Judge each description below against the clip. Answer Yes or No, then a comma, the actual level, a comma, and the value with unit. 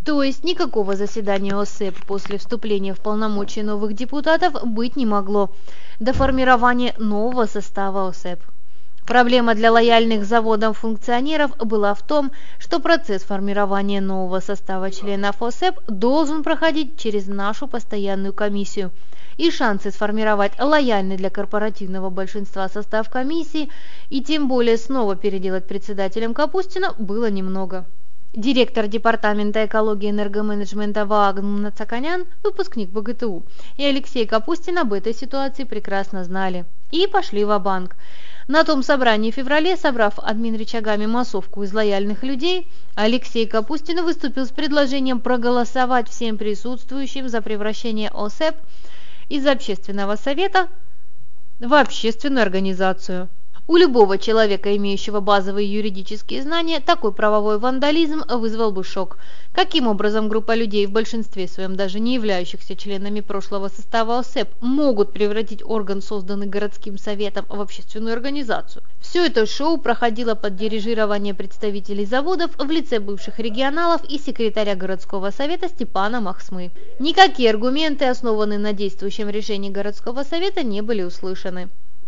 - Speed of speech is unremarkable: Yes, average, 125 wpm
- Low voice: No, high, 220 Hz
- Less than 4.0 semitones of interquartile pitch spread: No, average, 4.4 semitones